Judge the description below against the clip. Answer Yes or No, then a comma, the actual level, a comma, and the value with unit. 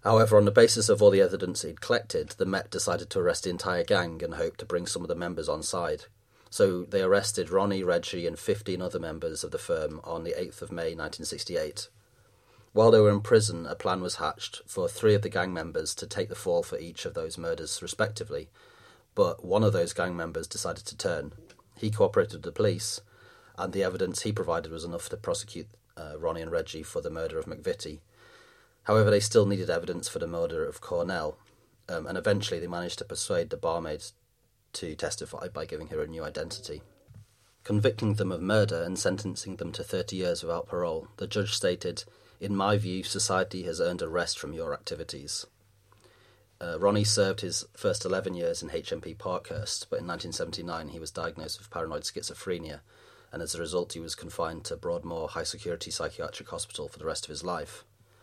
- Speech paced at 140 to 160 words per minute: No, average, 200 wpm